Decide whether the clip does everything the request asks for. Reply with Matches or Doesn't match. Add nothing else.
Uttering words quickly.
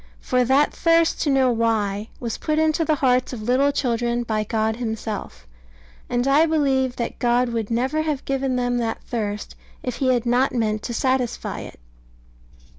Doesn't match